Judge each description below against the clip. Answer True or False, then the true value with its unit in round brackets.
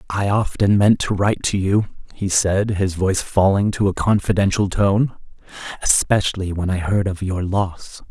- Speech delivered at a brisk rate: False (170 wpm)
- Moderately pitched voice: False (95 Hz)